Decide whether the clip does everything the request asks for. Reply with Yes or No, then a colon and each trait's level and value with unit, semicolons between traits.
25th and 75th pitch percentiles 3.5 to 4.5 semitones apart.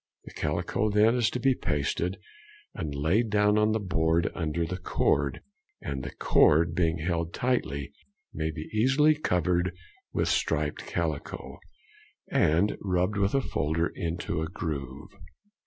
No: average, 4.9 semitones